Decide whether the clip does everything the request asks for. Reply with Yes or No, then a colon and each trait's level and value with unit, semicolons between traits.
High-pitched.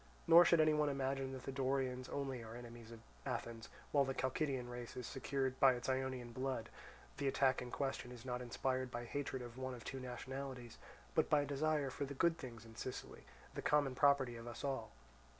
No: low, 130 Hz